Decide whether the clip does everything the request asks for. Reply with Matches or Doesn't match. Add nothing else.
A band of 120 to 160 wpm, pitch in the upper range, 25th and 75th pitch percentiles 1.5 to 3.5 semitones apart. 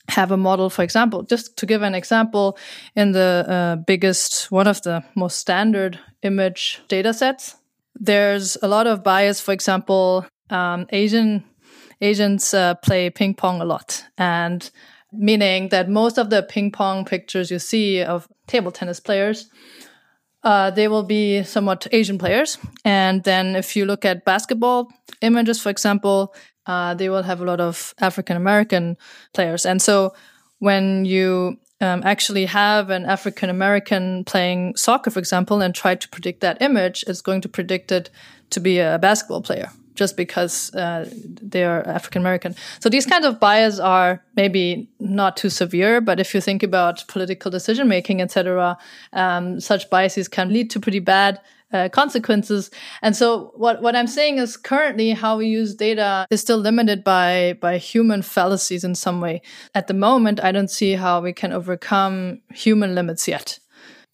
Doesn't match